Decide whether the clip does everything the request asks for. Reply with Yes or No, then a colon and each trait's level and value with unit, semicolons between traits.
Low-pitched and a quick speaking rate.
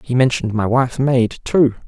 No: low, 125 Hz; average, 190 wpm